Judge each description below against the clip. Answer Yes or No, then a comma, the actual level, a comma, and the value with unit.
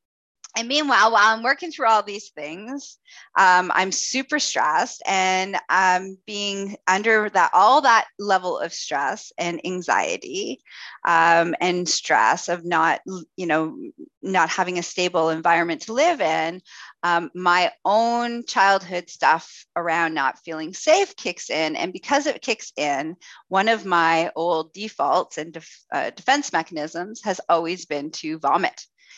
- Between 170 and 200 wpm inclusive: No, average, 145 wpm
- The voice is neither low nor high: Yes, medium, 180 Hz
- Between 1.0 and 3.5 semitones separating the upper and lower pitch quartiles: No, average, 4.9 semitones